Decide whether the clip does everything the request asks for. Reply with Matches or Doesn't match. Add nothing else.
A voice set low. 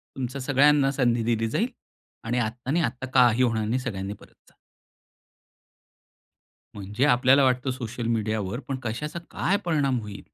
Matches